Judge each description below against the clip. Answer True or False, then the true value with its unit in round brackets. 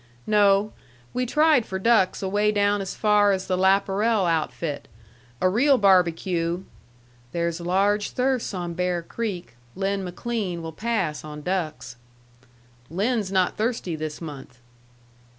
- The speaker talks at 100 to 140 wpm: True (135 wpm)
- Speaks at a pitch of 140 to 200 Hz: True (190 Hz)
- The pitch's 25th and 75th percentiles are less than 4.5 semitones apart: True (3.7 semitones)